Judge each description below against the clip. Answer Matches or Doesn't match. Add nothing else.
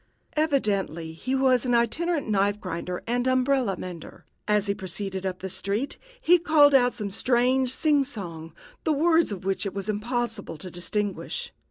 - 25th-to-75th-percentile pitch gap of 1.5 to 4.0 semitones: Doesn't match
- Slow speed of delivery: Doesn't match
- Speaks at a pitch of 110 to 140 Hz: Doesn't match